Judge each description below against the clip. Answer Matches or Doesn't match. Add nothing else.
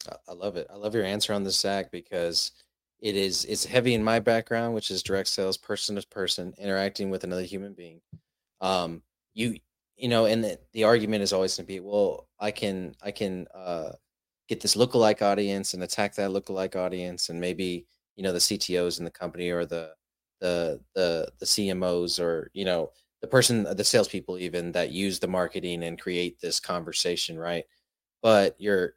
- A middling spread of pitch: Matches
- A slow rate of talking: Doesn't match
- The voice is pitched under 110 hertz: Matches